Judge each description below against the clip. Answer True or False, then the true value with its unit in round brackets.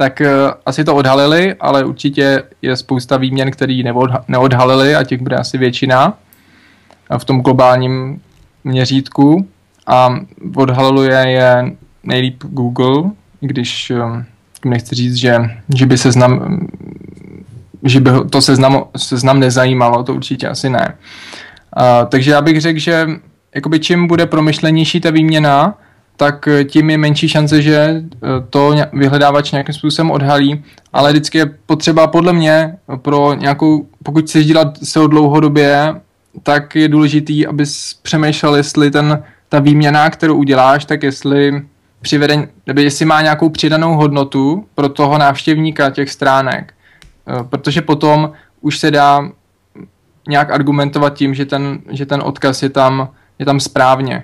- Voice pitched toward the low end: False (145 Hz)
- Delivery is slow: False (135 wpm)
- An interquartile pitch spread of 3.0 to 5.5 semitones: False (2.5 semitones)